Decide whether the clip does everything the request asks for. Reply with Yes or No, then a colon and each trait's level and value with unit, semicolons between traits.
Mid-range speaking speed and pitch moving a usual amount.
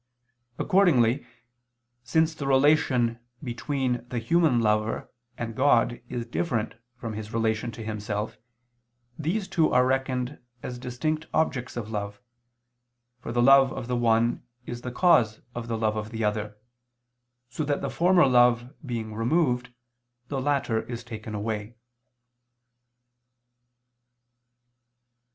No: slow, 125 wpm; average, 3.5 semitones